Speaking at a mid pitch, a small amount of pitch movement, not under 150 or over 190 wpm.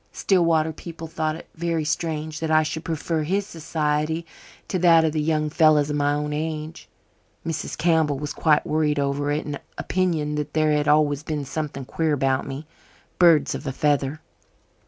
Yes: medium, 155 Hz; narrow, 1.5 semitones; average, 175 wpm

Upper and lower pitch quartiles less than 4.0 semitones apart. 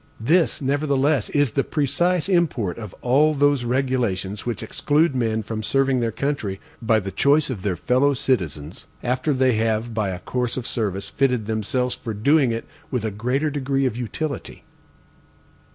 No: average, 4.3 semitones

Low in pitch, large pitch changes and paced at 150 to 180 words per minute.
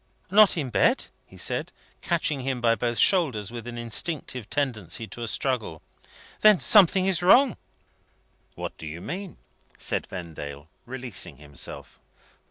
No: low, 120 Hz; wide, 8.2 semitones; average, 140 wpm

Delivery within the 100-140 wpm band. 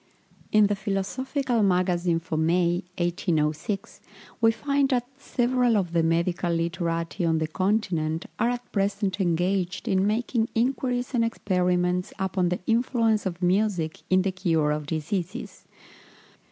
Yes: slow, 135 wpm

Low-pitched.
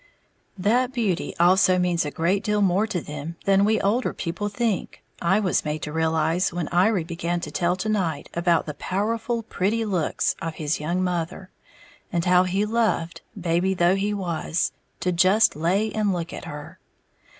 No: medium, 180 Hz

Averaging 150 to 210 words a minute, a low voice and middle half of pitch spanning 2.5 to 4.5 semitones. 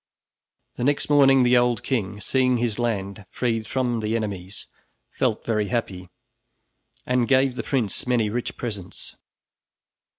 No: slow, 135 wpm; low, 120 Hz; average, 3.2 semitones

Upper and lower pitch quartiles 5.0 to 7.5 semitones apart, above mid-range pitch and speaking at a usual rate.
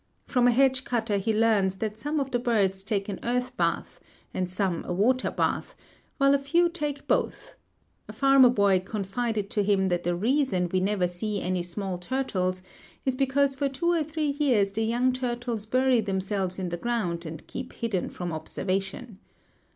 Yes: wide, 5.4 semitones; high, 220 Hz; average, 180 wpm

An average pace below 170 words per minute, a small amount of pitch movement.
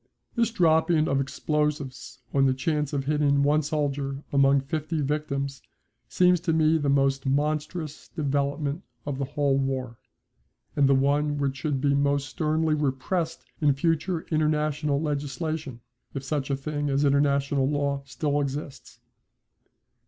Yes: average, 140 wpm; narrow, 1.8 semitones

